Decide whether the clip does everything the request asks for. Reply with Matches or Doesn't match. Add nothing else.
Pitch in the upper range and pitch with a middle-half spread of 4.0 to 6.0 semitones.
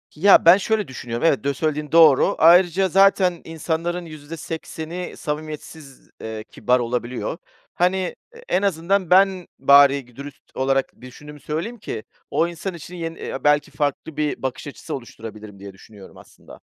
Doesn't match